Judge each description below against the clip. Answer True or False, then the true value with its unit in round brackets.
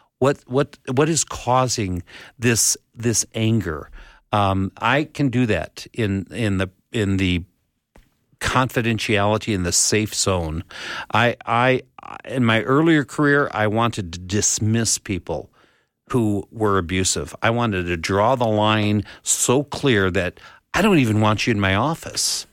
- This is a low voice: True (110 Hz)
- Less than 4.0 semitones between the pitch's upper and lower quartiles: False (4.5 semitones)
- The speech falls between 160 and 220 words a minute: False (145 wpm)